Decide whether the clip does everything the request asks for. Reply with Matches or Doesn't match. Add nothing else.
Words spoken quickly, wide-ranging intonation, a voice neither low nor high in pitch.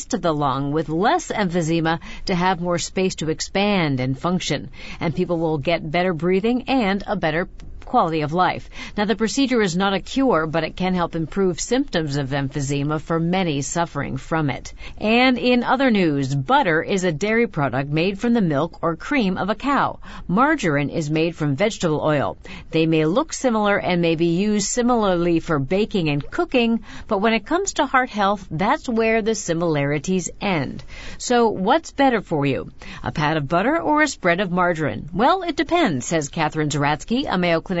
Doesn't match